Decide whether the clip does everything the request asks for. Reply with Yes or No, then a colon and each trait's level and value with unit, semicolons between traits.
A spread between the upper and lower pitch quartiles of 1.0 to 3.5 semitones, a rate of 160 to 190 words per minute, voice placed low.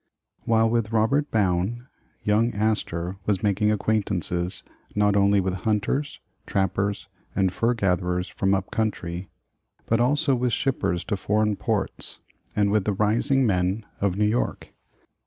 No: average, 2.8 semitones; average, 140 wpm; low, 105 Hz